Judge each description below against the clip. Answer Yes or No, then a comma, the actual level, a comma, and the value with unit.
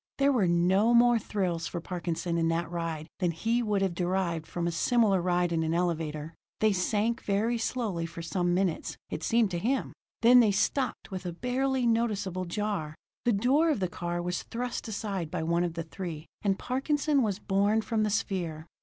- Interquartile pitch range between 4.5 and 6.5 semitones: Yes, average, 5.0 semitones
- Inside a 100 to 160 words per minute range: No, average, 195 wpm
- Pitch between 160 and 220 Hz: Yes, high, 190 Hz